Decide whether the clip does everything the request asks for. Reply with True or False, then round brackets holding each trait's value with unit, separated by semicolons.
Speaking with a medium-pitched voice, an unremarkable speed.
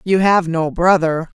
True (175 Hz; 175 wpm)